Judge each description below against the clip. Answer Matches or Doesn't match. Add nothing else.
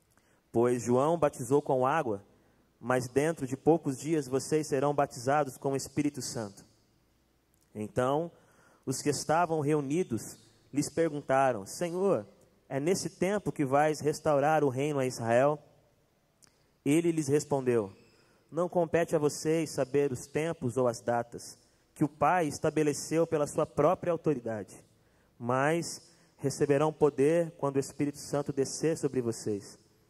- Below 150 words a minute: Matches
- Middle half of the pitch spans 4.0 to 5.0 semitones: Doesn't match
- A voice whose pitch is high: Doesn't match